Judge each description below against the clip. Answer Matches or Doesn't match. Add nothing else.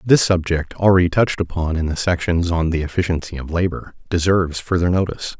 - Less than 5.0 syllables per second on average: Doesn't match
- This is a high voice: Doesn't match